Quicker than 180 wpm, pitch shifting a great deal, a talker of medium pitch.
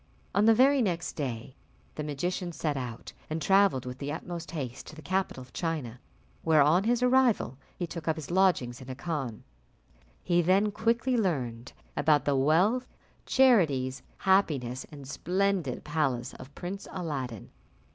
No: average, 155 wpm; wide, 6.4 semitones; medium, 160 Hz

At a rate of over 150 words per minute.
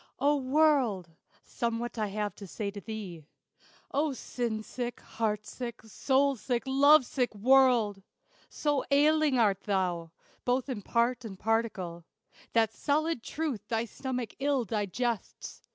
No: slow, 135 wpm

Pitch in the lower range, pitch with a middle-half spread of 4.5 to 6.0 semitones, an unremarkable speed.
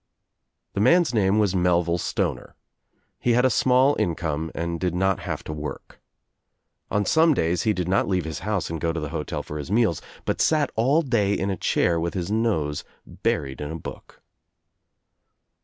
Yes: very low, 95 Hz; average, 5.2 semitones; average, 185 wpm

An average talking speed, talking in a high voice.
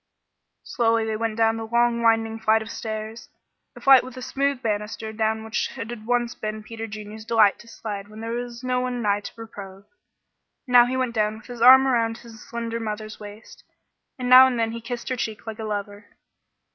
No: fast, 210 wpm; high, 225 Hz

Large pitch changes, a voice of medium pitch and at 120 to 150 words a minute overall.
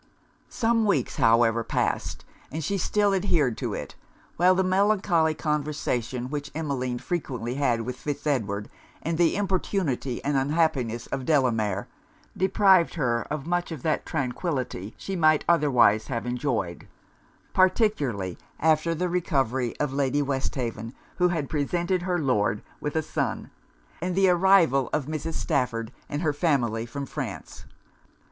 Yes: wide, 5.8 semitones; medium, 145 Hz; average, 140 wpm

